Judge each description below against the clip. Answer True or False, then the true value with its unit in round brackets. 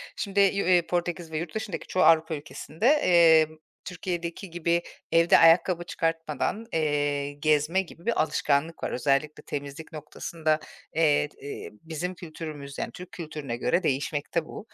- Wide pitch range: False (2.7 semitones)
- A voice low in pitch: False (165 Hz)